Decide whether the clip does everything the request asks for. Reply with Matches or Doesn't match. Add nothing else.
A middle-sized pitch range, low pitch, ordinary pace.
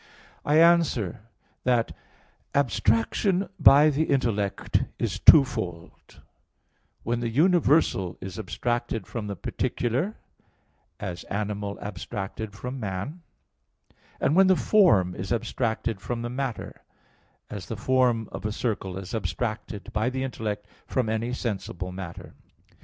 Doesn't match